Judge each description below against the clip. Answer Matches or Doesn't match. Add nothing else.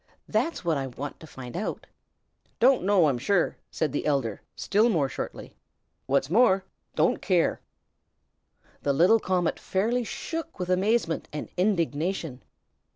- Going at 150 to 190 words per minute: Doesn't match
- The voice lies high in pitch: Doesn't match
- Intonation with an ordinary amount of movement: Doesn't match